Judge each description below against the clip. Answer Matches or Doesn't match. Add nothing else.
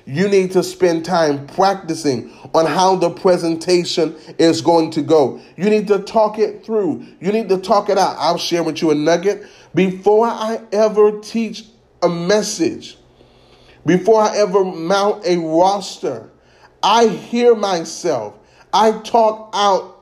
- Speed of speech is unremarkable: Matches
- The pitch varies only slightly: Doesn't match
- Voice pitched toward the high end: Matches